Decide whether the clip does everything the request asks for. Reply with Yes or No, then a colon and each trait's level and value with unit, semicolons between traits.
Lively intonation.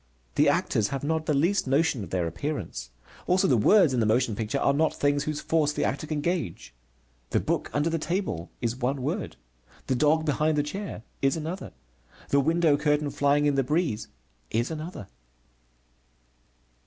No: average, 3.9 semitones